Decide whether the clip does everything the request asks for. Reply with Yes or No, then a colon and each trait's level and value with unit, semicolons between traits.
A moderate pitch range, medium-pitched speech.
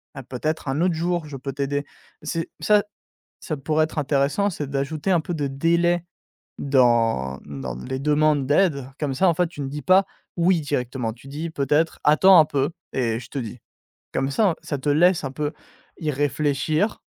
Yes: average, 3.5 semitones; medium, 145 Hz